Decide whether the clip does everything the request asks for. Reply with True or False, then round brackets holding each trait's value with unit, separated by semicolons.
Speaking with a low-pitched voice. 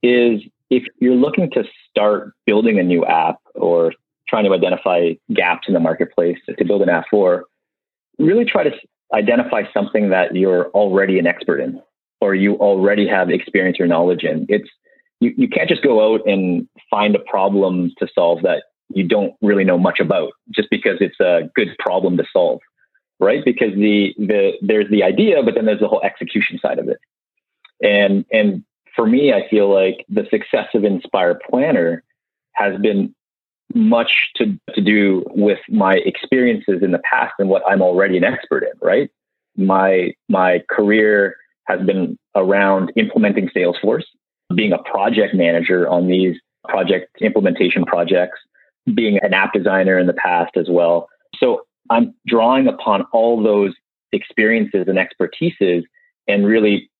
True (105 Hz)